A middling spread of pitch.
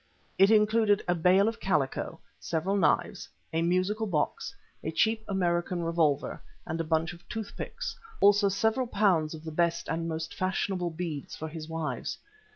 Yes: average, 3.8 semitones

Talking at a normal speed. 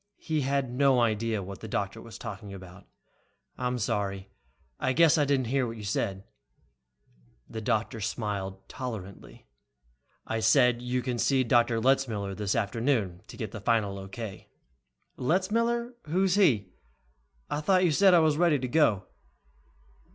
Yes: average, 150 wpm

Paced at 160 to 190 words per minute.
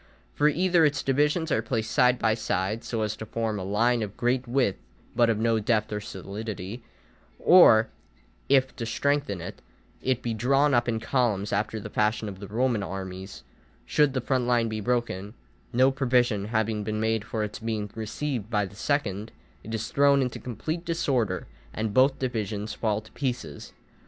Yes: average, 180 wpm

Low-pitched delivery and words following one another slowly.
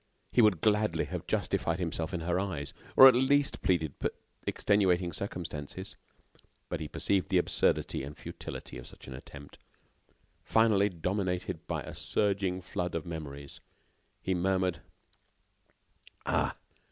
Yes: very low, 90 Hz; slow, 130 wpm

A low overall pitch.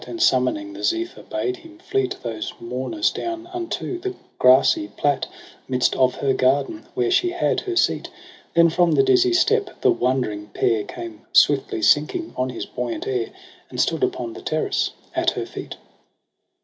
No: very high, 315 Hz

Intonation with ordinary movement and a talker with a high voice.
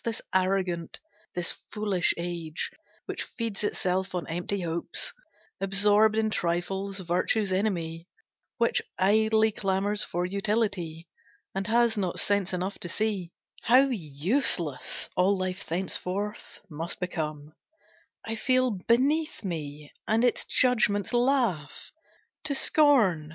Yes: average, 4.0 semitones; high, 195 Hz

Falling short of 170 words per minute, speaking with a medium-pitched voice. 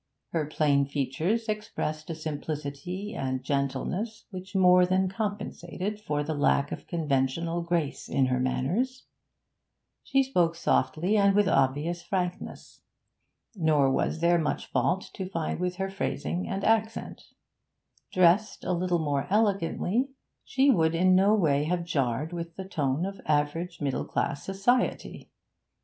Yes: average, 140 wpm; medium, 170 Hz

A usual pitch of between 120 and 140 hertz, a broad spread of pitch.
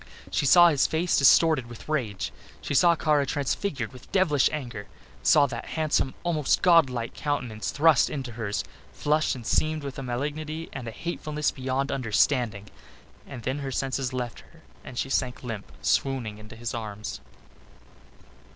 No: low, 135 Hz; average, 4.2 semitones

